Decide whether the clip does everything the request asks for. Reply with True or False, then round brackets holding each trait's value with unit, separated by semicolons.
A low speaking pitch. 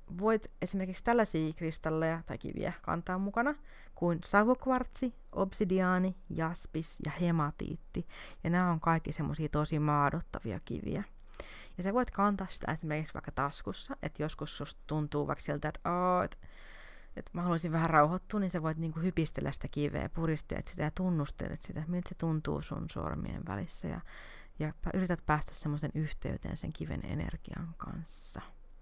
False (165 Hz)